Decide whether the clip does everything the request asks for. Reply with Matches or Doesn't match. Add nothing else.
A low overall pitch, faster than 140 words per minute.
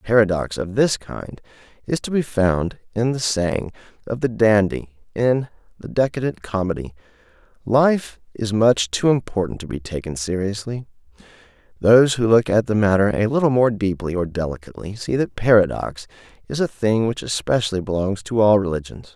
Matches